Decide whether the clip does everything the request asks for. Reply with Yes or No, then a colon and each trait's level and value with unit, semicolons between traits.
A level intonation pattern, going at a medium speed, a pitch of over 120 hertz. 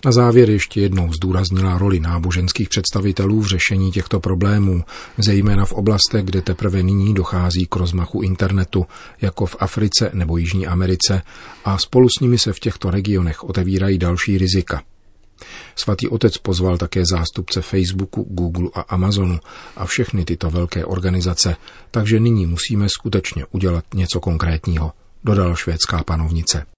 No: narrow, 2.2 semitones; average, 140 wpm; very low, 95 Hz